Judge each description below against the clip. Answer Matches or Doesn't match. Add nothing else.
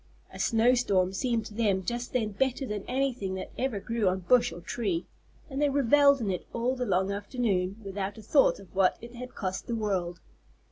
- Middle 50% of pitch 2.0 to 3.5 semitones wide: Doesn't match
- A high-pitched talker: Matches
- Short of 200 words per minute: Doesn't match